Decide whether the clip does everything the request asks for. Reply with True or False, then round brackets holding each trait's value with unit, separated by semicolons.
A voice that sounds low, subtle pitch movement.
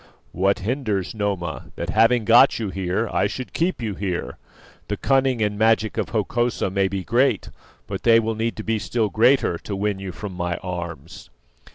False (105 Hz; 3.4 semitones)